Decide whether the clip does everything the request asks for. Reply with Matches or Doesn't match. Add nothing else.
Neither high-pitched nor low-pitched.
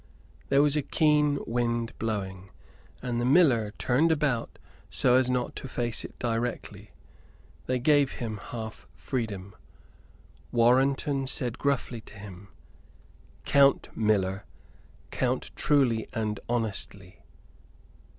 Doesn't match